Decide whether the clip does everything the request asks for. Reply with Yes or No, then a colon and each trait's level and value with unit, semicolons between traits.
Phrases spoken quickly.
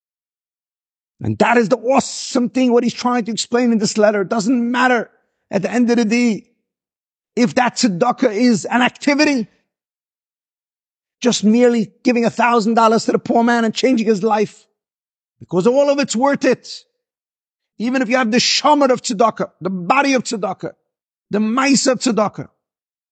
No: average, 170 wpm